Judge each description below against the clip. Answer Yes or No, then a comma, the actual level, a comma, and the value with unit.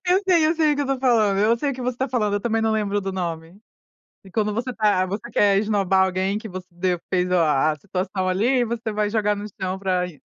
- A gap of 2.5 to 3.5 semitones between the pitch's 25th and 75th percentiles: No, average, 3.9 semitones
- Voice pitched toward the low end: No, high, 205 Hz